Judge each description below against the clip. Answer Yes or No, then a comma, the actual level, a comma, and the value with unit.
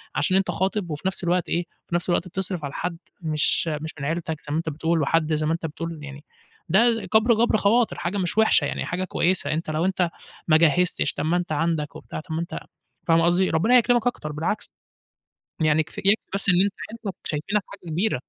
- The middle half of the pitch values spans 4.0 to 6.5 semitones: No, average, 3.4 semitones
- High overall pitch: No, medium, 170 Hz